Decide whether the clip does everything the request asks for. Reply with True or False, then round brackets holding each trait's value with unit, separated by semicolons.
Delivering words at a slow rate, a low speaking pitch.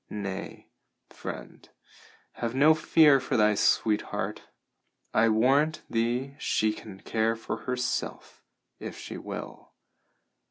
True (110 wpm; 115 Hz)